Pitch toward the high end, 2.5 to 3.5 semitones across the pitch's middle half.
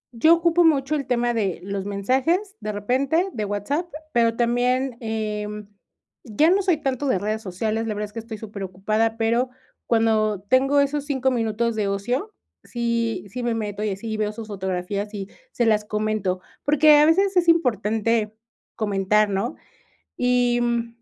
No: high, 230 Hz; average, 3.9 semitones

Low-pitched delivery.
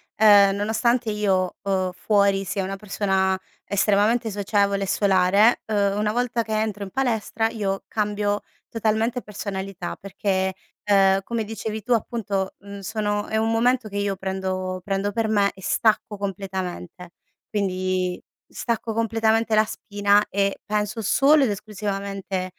No: high, 205 Hz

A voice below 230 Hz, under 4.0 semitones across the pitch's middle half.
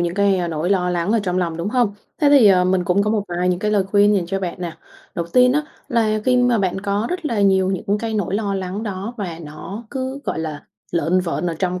Yes: high, 195 Hz; average, 3.2 semitones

